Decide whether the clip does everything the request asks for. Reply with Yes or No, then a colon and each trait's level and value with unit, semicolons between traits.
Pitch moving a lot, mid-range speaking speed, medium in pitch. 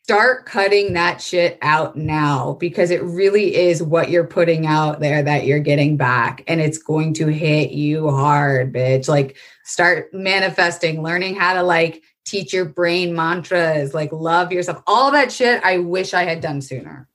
No: average, 3.0 semitones; average, 175 wpm; medium, 165 Hz